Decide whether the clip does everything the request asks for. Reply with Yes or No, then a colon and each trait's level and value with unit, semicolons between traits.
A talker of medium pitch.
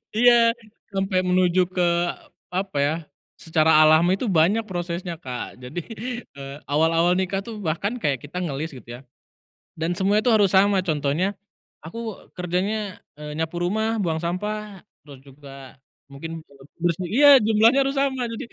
Yes: medium, 180 Hz